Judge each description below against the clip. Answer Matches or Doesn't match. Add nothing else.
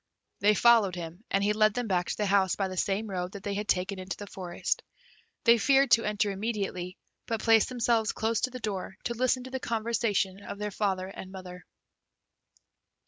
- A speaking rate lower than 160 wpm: Doesn't match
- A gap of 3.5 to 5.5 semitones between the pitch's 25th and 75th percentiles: Doesn't match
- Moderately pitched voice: Doesn't match